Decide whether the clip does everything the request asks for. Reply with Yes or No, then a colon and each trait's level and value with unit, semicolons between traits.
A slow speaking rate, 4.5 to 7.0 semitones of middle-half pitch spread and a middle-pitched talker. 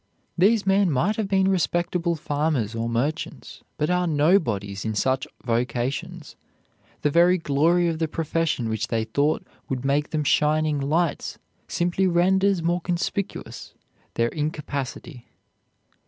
Yes: slow, 130 wpm; average, 4.8 semitones; medium, 155 Hz